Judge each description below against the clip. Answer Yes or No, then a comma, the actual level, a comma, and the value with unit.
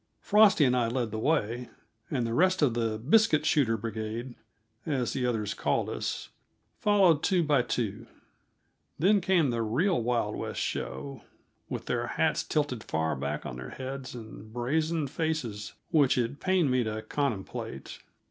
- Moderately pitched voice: No, low, 125 Hz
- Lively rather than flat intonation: Yes, wide, 5.9 semitones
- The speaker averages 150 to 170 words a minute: Yes, average, 155 wpm